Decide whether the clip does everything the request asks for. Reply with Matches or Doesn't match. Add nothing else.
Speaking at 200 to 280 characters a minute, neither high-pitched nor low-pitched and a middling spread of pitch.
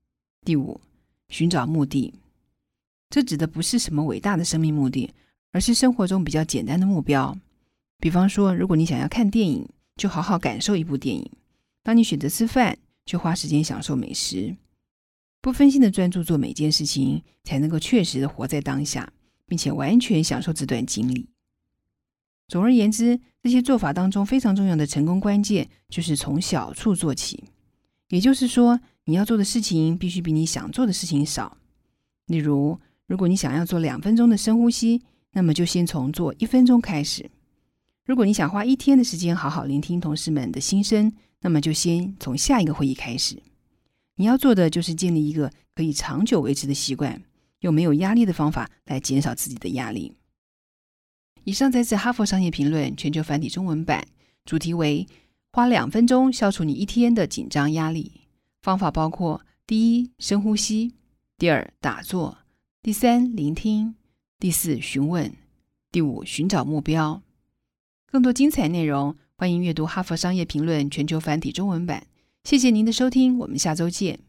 Doesn't match